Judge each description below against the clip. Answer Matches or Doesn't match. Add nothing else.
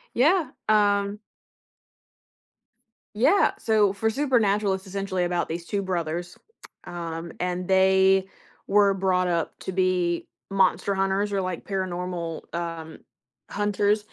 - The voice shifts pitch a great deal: Doesn't match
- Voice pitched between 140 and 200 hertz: Matches